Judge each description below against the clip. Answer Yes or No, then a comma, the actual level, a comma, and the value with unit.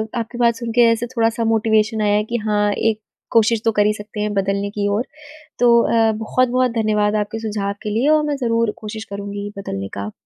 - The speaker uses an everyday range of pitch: No, narrow, 1.9 semitones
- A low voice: No, high, 220 Hz